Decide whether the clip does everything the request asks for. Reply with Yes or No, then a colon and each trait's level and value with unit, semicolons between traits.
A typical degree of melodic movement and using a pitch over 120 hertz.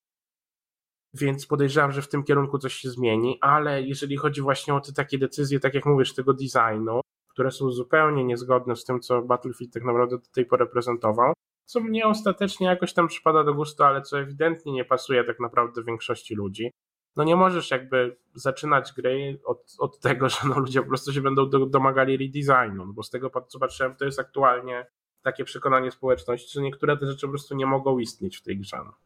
No: narrow, 2.2 semitones; low, 135 Hz